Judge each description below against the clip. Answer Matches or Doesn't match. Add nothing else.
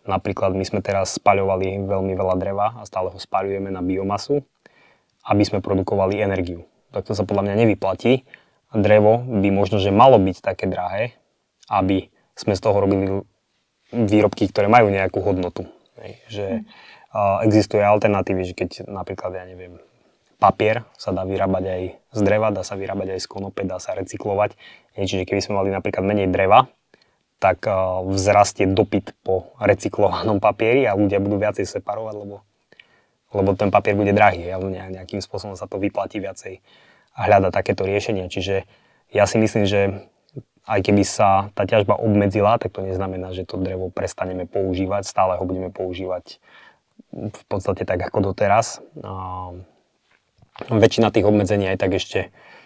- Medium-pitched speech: Doesn't match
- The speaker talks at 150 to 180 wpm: Matches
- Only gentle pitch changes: Matches